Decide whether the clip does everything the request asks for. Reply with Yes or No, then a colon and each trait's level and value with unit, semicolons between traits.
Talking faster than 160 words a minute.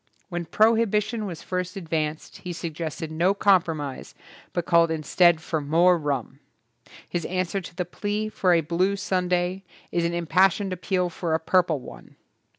No: average, 155 wpm